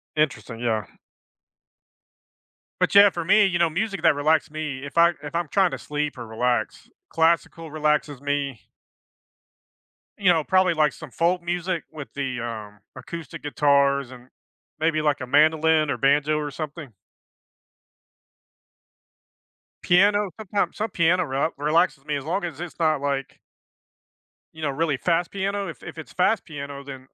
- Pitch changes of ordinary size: Yes, average, 3.5 semitones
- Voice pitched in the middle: Yes, medium, 155 Hz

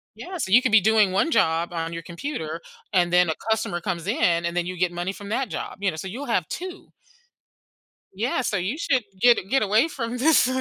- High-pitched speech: Yes, high, 200 Hz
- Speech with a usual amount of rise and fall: No, wide, 6.1 semitones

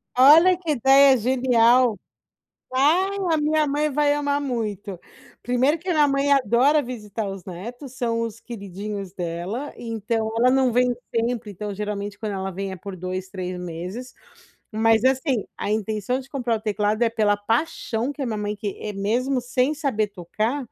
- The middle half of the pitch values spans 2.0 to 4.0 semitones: No, average, 4.5 semitones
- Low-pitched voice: No, high, 230 Hz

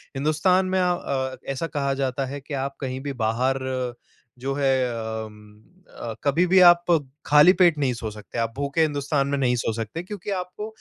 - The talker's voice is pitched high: No, medium, 140 Hz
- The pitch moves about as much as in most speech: Yes, average, 4.1 semitones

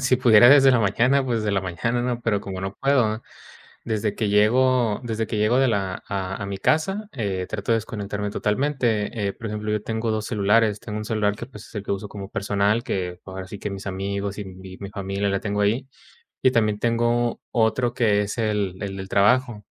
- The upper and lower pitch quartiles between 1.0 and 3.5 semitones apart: Yes, average, 2.9 semitones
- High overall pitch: No, low, 105 Hz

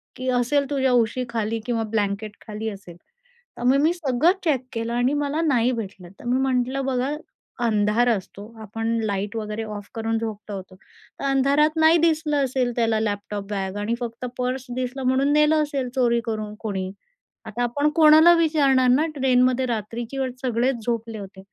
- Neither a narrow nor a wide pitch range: Yes, average, 3.8 semitones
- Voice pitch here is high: Yes, high, 245 Hz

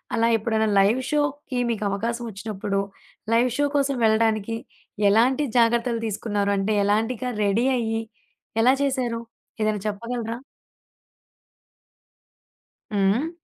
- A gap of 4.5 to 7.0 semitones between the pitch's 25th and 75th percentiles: No, average, 2.8 semitones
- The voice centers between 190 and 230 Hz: Yes, high, 225 Hz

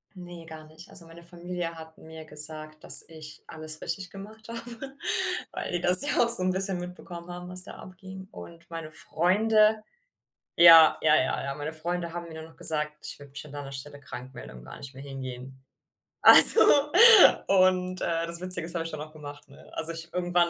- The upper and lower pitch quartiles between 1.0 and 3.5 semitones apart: Yes, average, 2.9 semitones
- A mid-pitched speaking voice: Yes, medium, 165 Hz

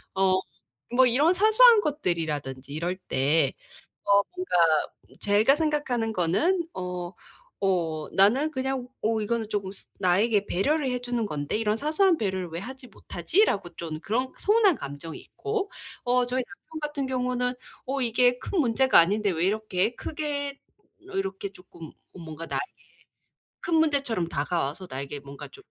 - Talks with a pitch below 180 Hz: No, high, 220 Hz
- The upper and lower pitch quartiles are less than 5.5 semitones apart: No, wide, 7.7 semitones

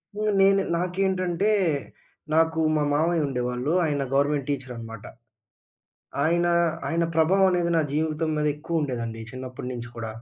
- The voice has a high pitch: No, medium, 155 Hz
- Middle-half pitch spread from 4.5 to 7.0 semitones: Yes, average, 5.1 semitones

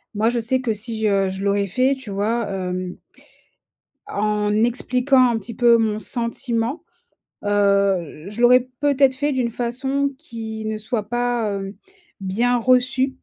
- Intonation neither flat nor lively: Yes, average, 3.6 semitones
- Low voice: No, high, 230 Hz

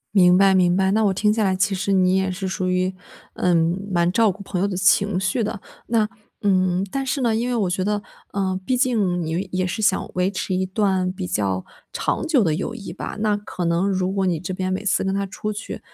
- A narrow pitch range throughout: Yes, narrow, 2.1 semitones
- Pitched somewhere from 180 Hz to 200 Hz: Yes, high, 190 Hz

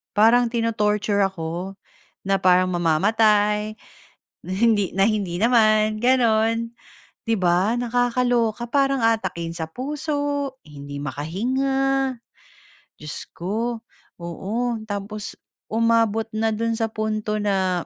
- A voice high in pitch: Yes, high, 215 Hz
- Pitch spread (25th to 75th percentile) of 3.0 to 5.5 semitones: Yes, average, 3.7 semitones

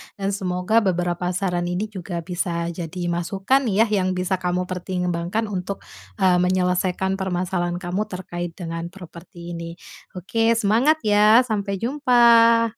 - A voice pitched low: No, medium, 185 Hz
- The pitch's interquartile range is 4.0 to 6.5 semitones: No, average, 3.0 semitones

